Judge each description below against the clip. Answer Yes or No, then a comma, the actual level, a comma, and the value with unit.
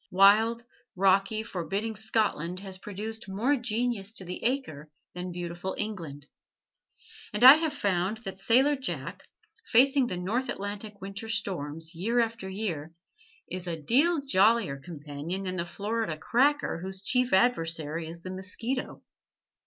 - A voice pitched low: No, high, 195 Hz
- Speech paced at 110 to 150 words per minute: Yes, slow, 135 wpm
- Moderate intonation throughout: Yes, average, 4.5 semitones